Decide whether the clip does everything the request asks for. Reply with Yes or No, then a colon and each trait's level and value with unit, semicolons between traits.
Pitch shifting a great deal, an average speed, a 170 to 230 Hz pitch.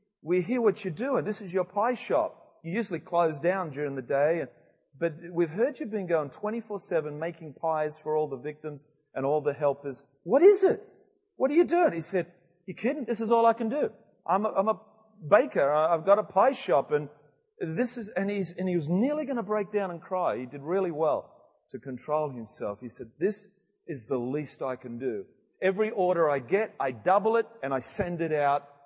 No: wide, 6.1 semitones; fast, 220 wpm; medium, 180 Hz